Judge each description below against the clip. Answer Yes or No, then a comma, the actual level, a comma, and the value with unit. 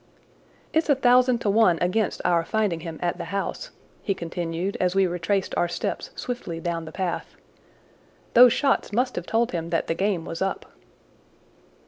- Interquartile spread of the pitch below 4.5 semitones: No, average, 4.9 semitones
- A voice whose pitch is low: No, medium, 185 Hz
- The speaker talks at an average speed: Yes, average, 170 wpm